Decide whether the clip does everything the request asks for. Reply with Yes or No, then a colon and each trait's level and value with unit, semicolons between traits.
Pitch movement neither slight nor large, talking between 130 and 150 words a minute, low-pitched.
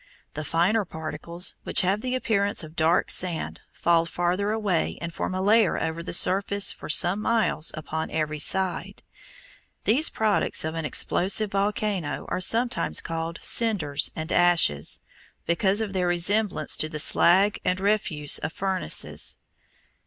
No: average, 3.9 semitones; average, 145 wpm; medium, 180 Hz